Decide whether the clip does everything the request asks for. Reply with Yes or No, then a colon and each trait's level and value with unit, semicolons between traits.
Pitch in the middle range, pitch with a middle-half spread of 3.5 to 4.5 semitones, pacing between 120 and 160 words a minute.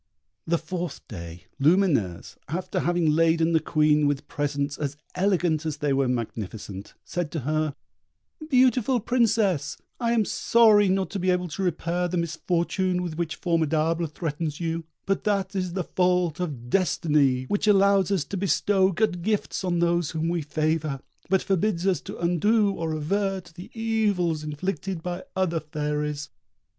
Yes: medium, 170 Hz; average, 3.9 semitones; average, 155 wpm